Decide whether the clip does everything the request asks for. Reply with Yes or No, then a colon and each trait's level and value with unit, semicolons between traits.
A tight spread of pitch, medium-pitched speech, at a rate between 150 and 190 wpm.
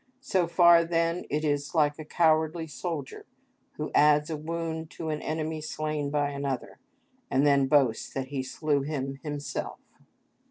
Yes: narrow, 2.1 semitones; medium, 150 Hz; average, 155 wpm